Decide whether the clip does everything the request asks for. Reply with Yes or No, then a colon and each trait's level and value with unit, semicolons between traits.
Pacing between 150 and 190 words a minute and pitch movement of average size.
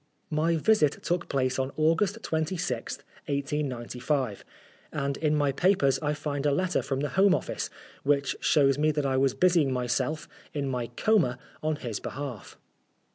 Yes: average, 155 wpm; average, 3.0 semitones